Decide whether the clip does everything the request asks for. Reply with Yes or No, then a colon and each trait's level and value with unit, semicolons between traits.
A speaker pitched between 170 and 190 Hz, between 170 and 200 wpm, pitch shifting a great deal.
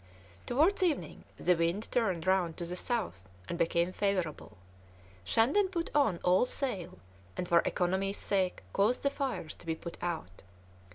No: medium, 185 Hz; average, 155 wpm; wide, 6.0 semitones